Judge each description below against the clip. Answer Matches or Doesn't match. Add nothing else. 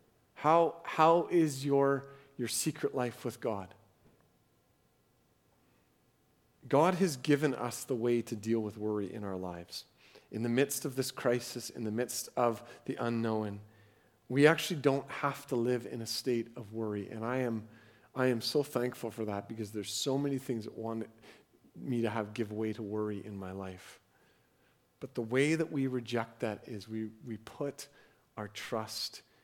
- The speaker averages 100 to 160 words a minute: Doesn't match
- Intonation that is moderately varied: Matches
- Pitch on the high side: Doesn't match